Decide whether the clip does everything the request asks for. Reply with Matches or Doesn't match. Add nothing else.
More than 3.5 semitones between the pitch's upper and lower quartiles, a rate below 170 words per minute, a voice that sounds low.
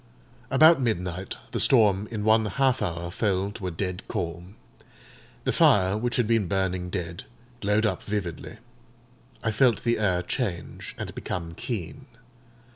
Matches